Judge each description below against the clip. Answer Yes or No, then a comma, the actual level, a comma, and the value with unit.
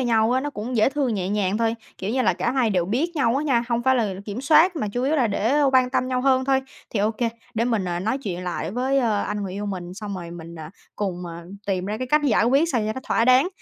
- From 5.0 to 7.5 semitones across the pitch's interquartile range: No, average, 4.6 semitones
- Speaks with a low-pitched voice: No, high, 230 Hz